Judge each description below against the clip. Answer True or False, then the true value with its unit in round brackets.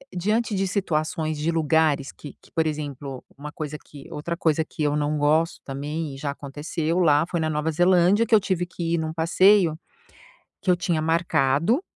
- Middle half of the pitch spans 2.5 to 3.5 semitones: True (2.9 semitones)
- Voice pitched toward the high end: False (160 Hz)